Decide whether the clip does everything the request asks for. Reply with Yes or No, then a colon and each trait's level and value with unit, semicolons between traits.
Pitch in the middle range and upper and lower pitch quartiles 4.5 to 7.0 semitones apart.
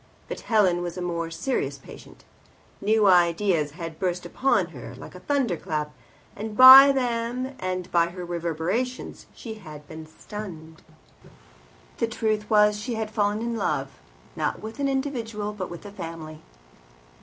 No: high, 200 Hz; average, 5.0 semitones